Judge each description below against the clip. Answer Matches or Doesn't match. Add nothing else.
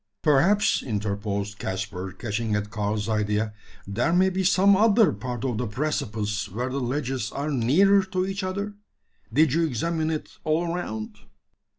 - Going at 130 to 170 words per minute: Matches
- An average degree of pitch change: Doesn't match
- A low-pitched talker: Matches